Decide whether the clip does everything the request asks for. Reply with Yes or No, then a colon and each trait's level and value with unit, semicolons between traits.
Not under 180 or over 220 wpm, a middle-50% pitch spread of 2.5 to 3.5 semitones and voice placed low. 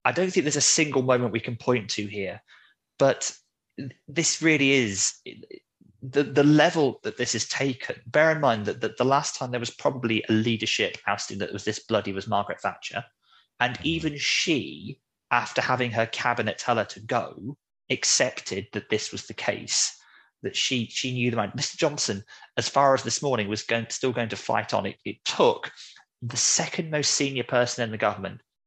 No: average, 195 wpm; average, 3.9 semitones; low, 125 Hz